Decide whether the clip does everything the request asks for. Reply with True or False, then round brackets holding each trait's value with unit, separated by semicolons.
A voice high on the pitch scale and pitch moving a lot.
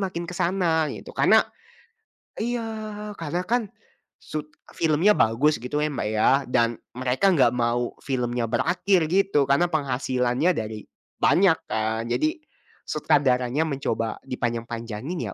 False (145 Hz; 6.9 semitones)